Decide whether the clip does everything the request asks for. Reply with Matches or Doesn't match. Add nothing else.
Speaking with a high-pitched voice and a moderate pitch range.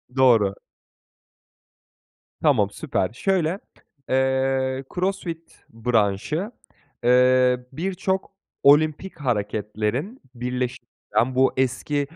Doesn't match